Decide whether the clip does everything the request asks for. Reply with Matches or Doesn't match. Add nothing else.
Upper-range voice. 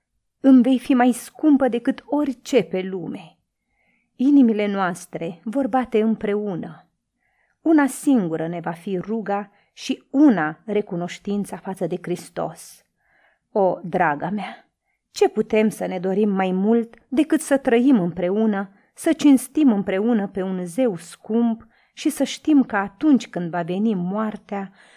Matches